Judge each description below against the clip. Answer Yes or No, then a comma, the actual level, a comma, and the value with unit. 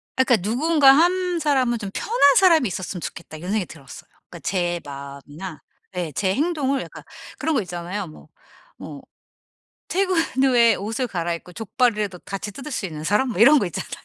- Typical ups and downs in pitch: No, wide, 7.7 semitones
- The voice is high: Yes, high, 215 Hz